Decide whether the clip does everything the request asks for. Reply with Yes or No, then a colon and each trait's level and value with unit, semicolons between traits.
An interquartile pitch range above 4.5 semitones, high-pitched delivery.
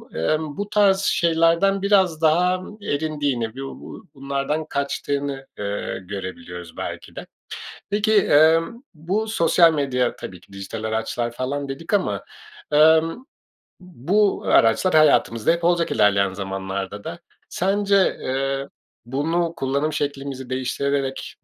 No: wide, 5.4 semitones; medium, 145 Hz